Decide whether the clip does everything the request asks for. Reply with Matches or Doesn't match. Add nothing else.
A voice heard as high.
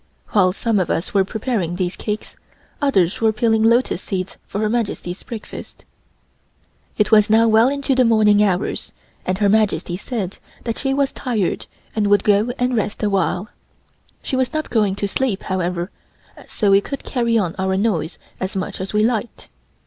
Matches